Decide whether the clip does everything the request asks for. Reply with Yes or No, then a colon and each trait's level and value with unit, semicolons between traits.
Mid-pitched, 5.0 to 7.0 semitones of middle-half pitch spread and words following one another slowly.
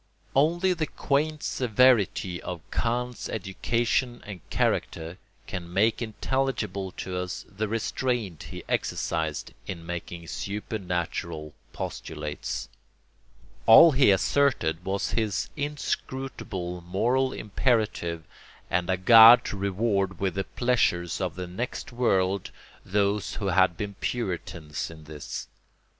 No: low, 100 Hz; wide, 5.4 semitones; slow, 115 wpm